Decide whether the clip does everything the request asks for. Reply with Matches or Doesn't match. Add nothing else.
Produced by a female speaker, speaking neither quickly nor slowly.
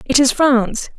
Matches